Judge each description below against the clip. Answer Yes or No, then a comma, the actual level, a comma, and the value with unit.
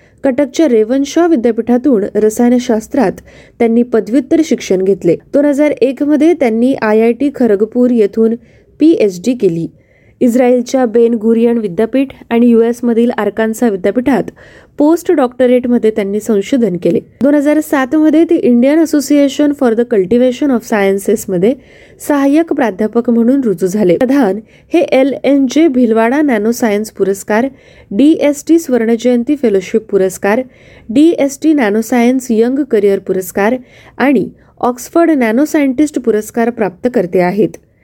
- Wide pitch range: No, average, 4.3 semitones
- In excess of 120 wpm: Yes, fast, 130 wpm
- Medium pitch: No, high, 240 Hz